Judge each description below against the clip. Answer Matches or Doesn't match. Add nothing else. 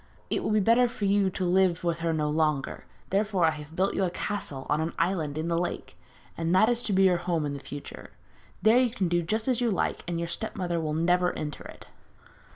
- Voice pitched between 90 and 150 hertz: Doesn't match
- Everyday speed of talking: Doesn't match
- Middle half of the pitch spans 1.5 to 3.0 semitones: Doesn't match